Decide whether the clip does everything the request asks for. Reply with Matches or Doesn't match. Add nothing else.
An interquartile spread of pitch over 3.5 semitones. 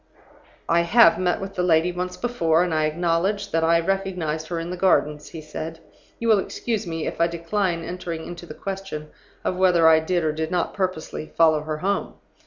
Doesn't match